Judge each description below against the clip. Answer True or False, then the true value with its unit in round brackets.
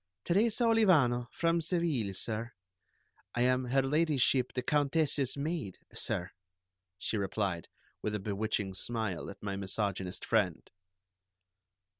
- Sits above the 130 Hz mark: False (120 Hz)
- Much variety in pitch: True (7.3 semitones)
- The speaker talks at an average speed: False (115 wpm)